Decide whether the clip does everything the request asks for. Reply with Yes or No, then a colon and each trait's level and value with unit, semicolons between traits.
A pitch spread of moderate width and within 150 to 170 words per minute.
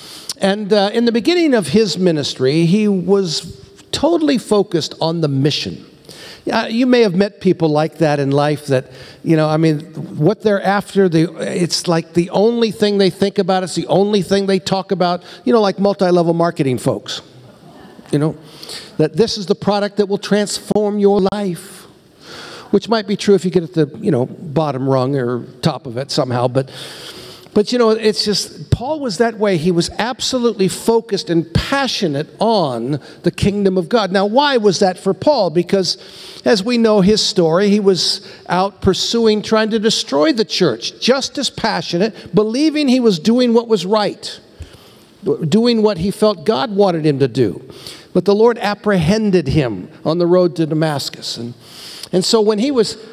No: average, 4.7 semitones; average, 185 wpm